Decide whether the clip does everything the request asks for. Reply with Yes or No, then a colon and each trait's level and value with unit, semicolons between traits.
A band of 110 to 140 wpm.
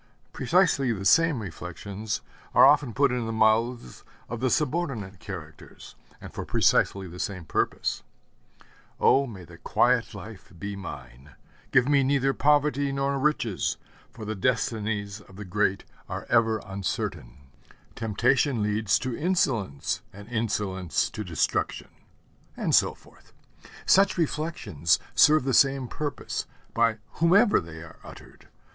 Yes: slow, 135 wpm